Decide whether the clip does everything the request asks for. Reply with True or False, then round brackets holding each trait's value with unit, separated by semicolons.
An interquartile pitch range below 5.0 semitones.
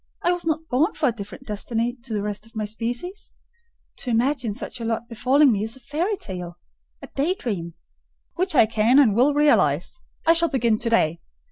False (5.6 semitones)